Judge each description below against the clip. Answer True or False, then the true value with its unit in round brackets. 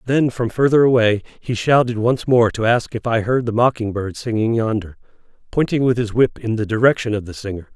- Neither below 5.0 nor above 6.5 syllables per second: True (5.5 syllables/s)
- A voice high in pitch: False (115 Hz)